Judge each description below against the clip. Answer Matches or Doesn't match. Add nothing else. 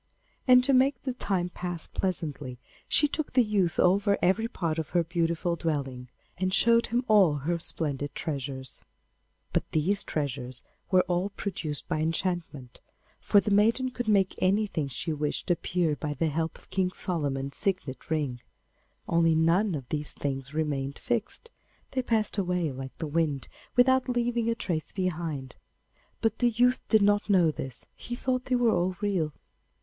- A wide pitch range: Matches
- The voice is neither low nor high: Matches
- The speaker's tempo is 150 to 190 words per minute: Matches